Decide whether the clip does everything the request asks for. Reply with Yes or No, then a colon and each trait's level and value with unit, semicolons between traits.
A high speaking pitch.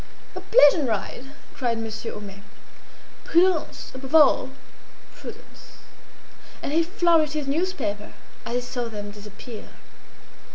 Yes: very high, 260 Hz